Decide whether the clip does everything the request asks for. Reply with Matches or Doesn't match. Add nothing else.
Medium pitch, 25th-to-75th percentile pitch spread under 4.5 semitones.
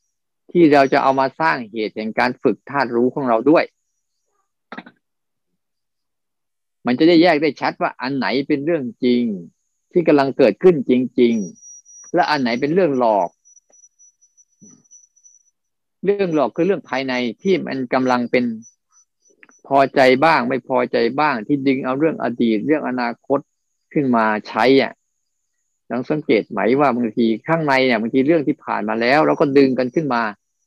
Doesn't match